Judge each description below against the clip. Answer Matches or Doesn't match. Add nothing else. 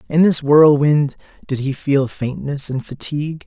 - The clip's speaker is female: Doesn't match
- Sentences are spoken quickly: Doesn't match